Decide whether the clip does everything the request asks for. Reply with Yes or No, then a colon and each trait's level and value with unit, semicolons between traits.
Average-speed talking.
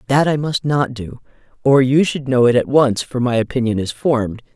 No: fast, 225 wpm